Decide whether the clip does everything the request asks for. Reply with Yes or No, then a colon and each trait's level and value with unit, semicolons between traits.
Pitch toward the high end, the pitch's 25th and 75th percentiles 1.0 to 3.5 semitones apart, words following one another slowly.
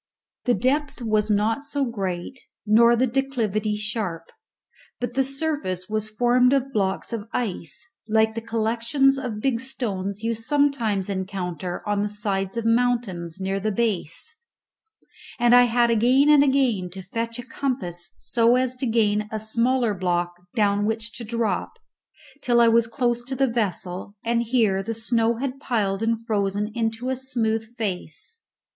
No: high, 225 Hz; average, 3.2 semitones; average, 155 wpm